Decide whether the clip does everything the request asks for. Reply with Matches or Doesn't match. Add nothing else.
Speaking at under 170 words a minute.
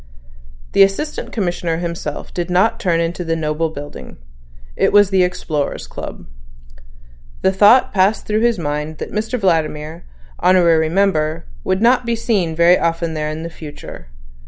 Matches